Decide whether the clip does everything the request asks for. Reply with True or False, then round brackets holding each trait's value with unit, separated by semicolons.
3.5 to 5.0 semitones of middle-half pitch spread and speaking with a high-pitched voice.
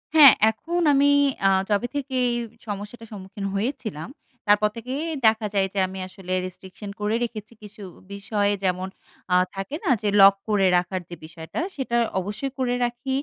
True (3.9 semitones; 210 Hz)